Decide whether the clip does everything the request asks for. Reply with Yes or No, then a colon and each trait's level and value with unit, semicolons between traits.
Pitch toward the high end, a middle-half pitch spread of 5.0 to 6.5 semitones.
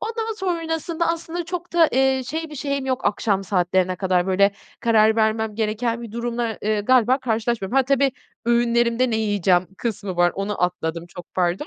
Yes: high, 230 Hz; wide, 5.6 semitones